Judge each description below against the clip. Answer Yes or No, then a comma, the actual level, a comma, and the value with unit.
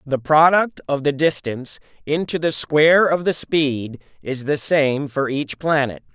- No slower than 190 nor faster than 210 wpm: No, average, 165 wpm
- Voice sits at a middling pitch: Yes, medium, 145 Hz